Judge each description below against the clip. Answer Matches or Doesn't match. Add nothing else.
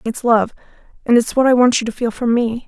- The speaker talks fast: Matches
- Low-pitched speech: Doesn't match